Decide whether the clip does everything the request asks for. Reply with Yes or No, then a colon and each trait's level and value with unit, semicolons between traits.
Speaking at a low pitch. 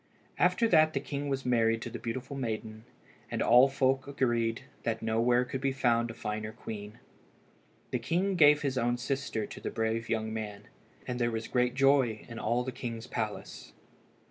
Yes: low, 120 Hz